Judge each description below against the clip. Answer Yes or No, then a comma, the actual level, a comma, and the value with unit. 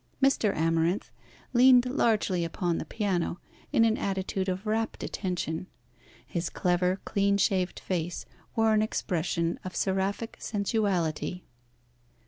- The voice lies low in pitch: No, high, 190 Hz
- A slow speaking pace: Yes, slow, 115 wpm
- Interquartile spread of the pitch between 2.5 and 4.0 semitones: Yes, average, 3.6 semitones